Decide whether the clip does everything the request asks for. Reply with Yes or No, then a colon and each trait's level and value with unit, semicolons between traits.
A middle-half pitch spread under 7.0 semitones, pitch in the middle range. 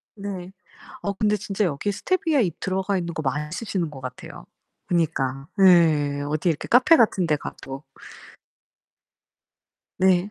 Yes: average, 5.1 semitones; medium, 175 Hz